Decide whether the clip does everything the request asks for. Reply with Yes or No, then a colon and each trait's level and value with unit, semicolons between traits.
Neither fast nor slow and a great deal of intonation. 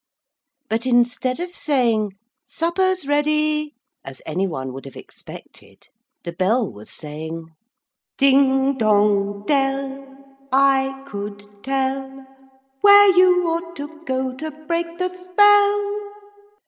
No: slow, 110 wpm; wide, 7.6 semitones